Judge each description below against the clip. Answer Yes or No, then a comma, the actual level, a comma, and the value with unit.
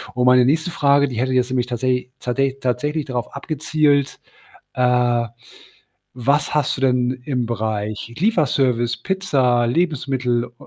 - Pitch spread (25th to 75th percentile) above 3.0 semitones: No, narrow, 2.6 semitones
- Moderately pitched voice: No, low, 130 Hz